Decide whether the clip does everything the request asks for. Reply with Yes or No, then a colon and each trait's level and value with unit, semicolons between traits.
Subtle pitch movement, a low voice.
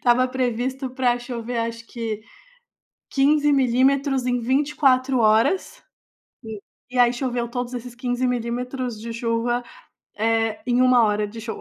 No: narrow, 1.9 semitones; high, 245 Hz